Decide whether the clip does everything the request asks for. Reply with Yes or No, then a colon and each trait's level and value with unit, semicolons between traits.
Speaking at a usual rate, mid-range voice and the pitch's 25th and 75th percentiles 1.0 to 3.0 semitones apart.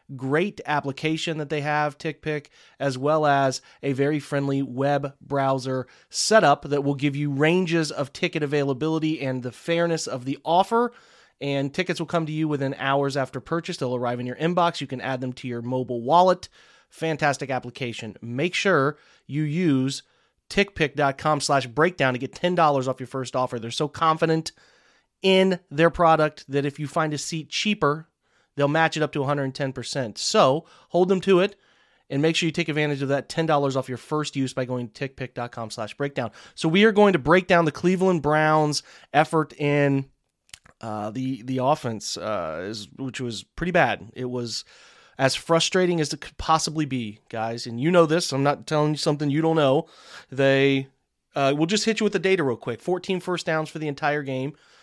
No: average, 190 wpm; medium, 145 Hz; average, 3.4 semitones